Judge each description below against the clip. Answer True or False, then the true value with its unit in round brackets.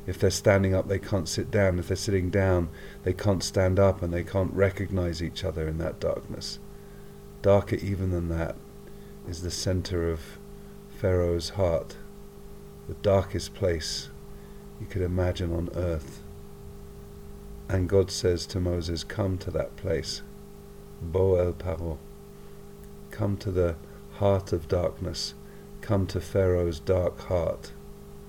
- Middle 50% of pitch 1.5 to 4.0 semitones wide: True (2.9 semitones)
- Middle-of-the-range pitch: False (90 Hz)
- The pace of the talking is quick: False (140 wpm)